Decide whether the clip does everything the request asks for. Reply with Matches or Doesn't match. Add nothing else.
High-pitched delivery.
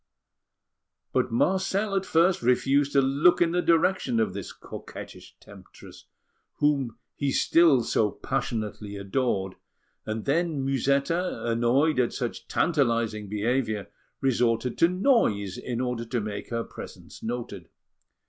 Doesn't match